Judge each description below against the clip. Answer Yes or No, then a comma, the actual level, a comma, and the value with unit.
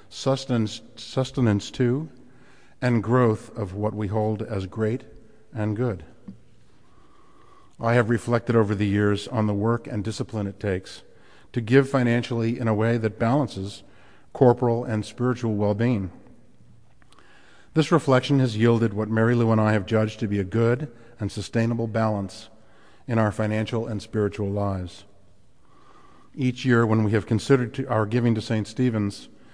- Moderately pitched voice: No, low, 115 Hz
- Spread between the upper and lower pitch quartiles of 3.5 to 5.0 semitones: No, narrow, 2.4 semitones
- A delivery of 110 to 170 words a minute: Yes, average, 150 wpm